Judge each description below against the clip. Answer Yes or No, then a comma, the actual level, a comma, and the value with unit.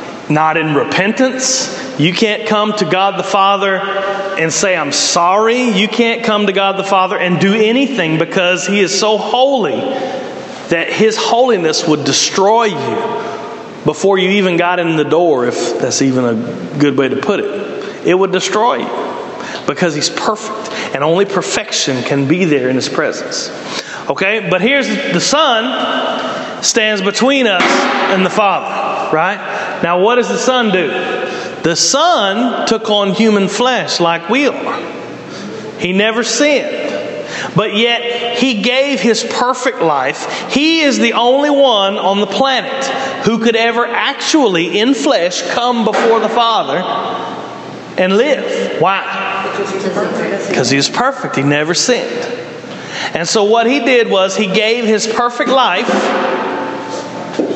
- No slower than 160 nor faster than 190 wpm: No, average, 150 wpm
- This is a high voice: Yes, high, 215 Hz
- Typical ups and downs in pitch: Yes, average, 4.2 semitones